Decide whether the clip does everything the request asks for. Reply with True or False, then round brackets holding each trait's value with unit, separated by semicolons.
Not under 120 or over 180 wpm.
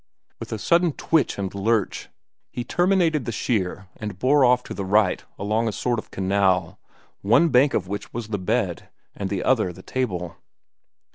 True (170 wpm)